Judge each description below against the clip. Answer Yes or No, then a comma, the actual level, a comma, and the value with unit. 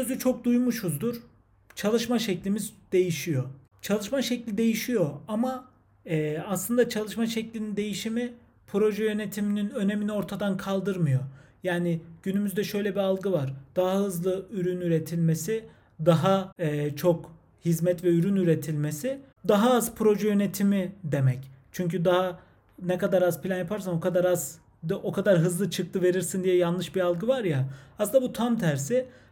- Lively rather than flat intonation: No, average, 3.8 semitones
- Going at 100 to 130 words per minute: No, fast, 140 wpm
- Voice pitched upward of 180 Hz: Yes, high, 190 Hz